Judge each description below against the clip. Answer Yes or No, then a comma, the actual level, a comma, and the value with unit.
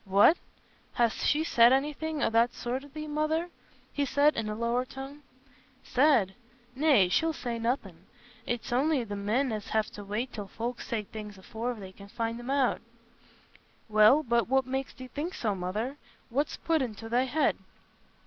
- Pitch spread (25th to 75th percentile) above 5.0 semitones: No, average, 4.7 semitones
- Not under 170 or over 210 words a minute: Yes, average, 175 wpm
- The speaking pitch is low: No, high, 245 Hz